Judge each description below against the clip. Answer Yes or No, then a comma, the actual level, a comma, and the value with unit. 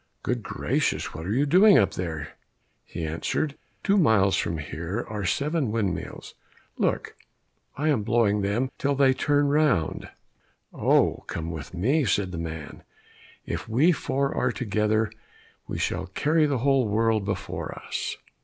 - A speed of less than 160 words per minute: Yes, average, 150 wpm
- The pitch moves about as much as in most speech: No, wide, 6.9 semitones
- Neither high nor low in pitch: No, low, 110 Hz